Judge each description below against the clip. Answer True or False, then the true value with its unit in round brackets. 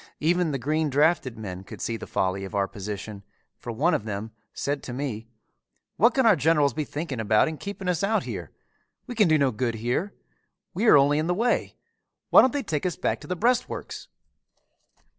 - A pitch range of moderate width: False (7.9 semitones)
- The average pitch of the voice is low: False (145 Hz)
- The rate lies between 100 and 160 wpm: False (205 wpm)